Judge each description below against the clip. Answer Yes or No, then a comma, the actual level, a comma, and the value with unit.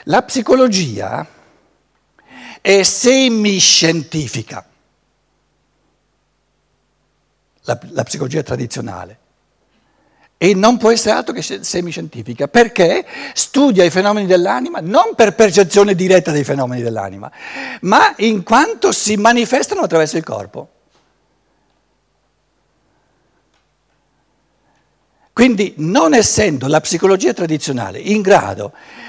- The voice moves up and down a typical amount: No, wide, 7.9 semitones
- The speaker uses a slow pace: Yes, slow, 85 wpm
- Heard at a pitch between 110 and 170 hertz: No, medium, 185 Hz